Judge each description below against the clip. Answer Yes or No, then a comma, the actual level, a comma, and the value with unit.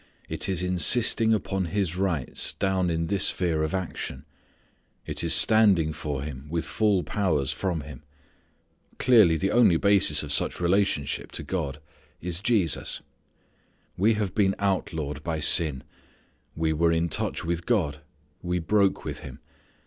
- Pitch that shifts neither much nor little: Yes, average, 4.0 semitones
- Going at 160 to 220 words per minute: No, average, 150 wpm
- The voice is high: No, very low, 90 Hz